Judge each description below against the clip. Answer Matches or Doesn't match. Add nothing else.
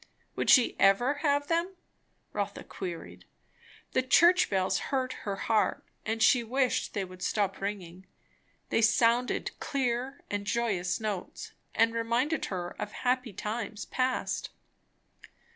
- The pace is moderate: Doesn't match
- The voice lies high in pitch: Matches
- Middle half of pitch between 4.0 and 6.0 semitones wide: Matches